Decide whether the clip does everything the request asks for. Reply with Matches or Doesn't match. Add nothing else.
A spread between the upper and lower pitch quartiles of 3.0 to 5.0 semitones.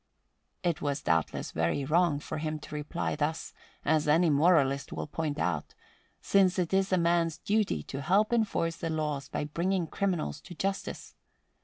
Matches